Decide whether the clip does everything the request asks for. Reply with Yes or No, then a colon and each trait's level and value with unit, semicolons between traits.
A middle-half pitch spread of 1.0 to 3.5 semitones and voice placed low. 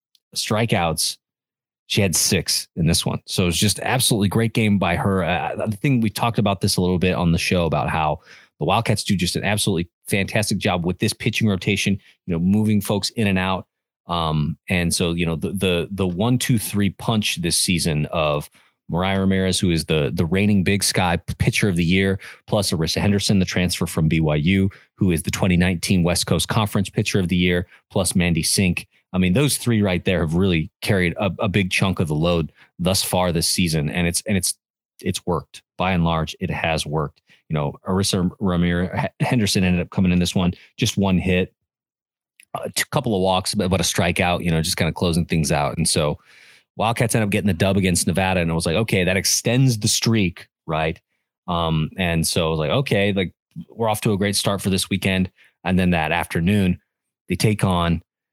Yes: average, 3.1 semitones; very low, 95 Hz